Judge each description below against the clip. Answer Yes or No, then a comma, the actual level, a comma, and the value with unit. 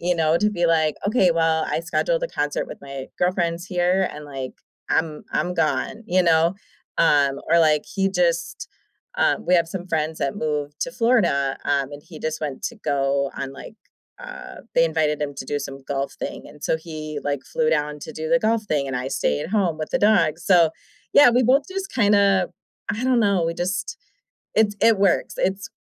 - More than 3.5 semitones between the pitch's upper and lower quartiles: Yes, average, 4.7 semitones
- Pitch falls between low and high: Yes, medium, 165 Hz